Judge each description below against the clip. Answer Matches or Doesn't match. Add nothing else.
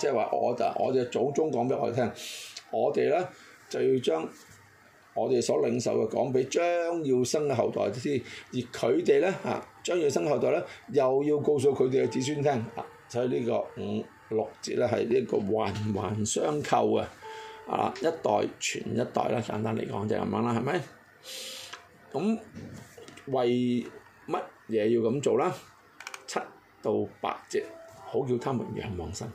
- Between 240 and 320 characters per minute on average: Doesn't match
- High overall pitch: Doesn't match